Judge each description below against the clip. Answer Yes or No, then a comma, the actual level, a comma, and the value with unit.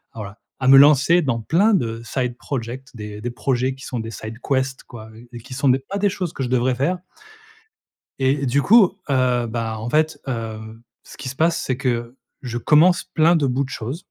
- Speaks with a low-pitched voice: Yes, low, 130 Hz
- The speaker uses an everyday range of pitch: Yes, average, 3.5 semitones